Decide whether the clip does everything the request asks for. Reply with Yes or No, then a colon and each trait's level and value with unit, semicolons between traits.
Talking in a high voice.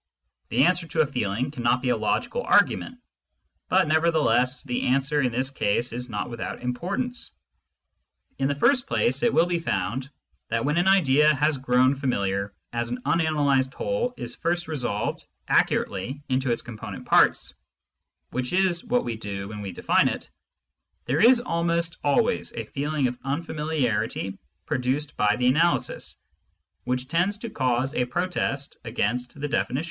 No: low, 135 Hz